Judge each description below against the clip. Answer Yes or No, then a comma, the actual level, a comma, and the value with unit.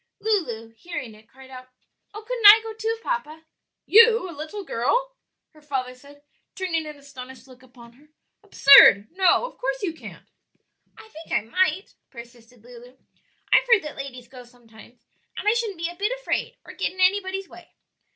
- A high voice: Yes, very high, 300 Hz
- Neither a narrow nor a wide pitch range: No, wide, 8.3 semitones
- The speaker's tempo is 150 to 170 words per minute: No, average, 180 wpm